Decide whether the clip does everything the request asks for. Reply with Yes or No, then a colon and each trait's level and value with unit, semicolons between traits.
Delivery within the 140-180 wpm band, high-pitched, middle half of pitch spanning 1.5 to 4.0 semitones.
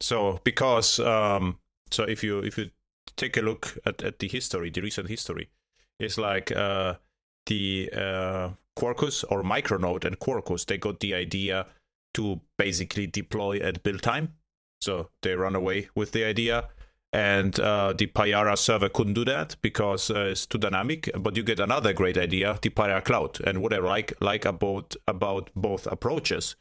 No: average, 170 wpm; low, 100 Hz; narrow, 2.5 semitones